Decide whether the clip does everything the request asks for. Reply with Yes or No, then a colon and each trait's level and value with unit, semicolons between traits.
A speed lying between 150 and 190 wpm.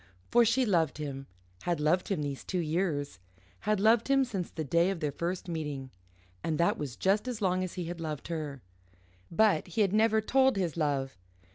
No: average, 200 wpm